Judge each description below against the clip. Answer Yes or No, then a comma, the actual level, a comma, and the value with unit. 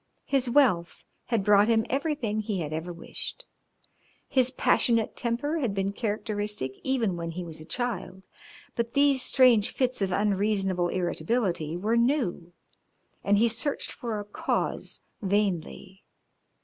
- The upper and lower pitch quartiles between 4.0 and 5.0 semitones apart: Yes, average, 4.6 semitones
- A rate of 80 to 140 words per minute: Yes, slow, 135 wpm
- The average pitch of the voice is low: No, high, 210 Hz